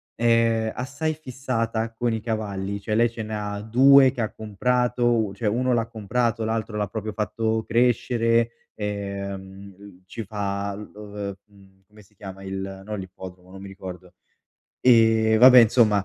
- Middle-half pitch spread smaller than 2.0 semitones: No, average, 2.7 semitones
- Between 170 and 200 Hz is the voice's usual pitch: No, low, 110 Hz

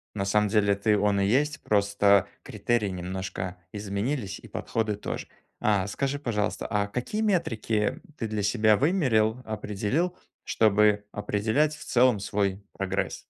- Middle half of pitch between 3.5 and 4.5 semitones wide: No, average, 2.9 semitones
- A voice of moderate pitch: No, low, 105 Hz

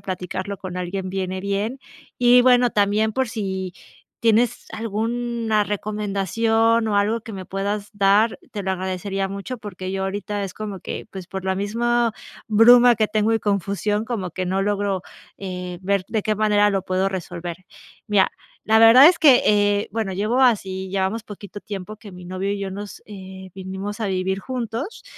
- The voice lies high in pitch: Yes, high, 205 Hz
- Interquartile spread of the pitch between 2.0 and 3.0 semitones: Yes, average, 2.7 semitones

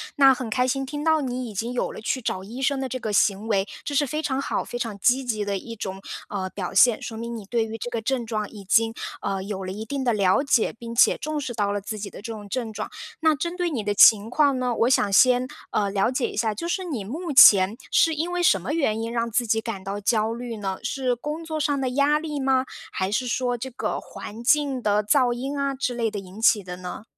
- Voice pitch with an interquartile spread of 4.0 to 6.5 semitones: Yes, average, 4.5 semitones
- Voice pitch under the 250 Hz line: Yes, high, 235 Hz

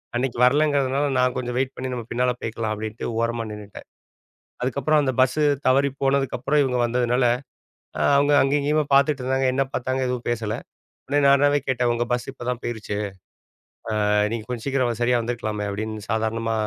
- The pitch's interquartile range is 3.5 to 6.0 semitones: No, average, 2.7 semitones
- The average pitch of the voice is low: Yes, low, 125 Hz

